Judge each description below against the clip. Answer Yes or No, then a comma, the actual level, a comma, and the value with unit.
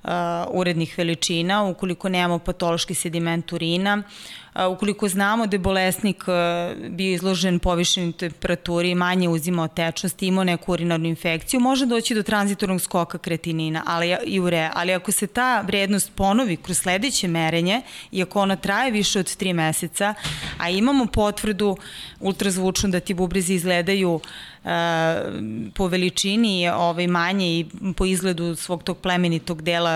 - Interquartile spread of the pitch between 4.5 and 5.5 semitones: No, narrow, 2.6 semitones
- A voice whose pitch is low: No, medium, 180 Hz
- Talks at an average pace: Yes, average, 140 wpm